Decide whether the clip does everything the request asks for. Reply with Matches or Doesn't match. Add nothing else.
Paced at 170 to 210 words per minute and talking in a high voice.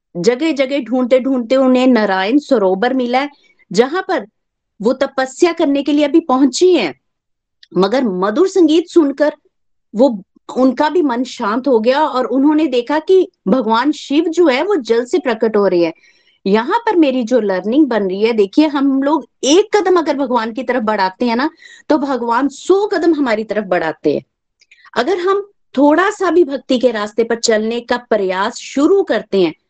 Matches